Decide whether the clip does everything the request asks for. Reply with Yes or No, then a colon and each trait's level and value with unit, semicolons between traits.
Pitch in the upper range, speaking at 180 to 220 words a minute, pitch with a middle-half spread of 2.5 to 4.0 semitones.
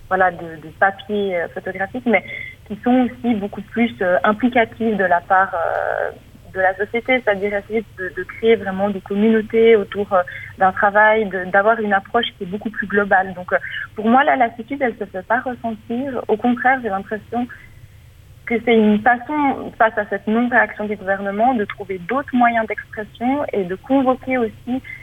Yes: high, 210 Hz; average, 185 wpm; average, 3.6 semitones